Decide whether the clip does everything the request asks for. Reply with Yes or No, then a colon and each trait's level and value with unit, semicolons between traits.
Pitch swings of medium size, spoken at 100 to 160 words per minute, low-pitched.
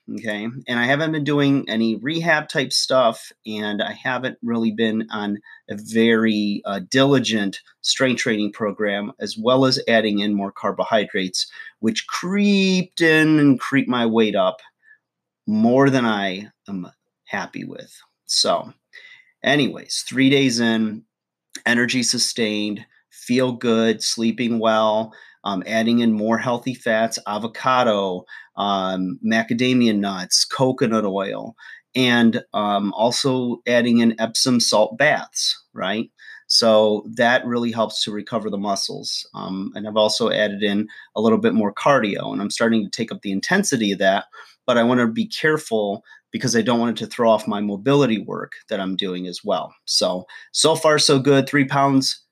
Yes: average, 3.9 semitones; average, 155 wpm; low, 115 Hz